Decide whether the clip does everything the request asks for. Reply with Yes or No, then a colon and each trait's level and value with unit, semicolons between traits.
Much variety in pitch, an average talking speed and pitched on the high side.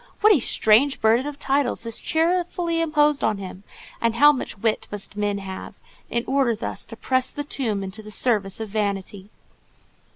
Yes: wide, 5.7 semitones; average, 175 wpm; high, 230 Hz